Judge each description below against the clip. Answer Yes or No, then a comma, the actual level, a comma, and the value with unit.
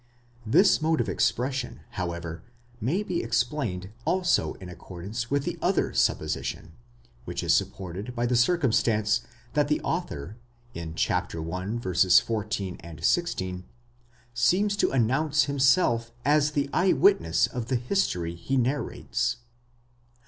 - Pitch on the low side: Yes, low, 120 Hz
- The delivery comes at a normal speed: No, slow, 125 wpm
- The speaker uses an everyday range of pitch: No, wide, 7.7 semitones